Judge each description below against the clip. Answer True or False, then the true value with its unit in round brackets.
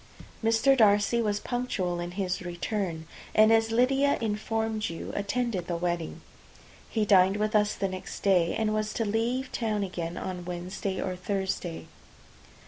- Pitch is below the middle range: False (205 Hz)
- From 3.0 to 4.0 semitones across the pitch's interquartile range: True (3.5 semitones)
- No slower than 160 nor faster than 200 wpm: False (150 wpm)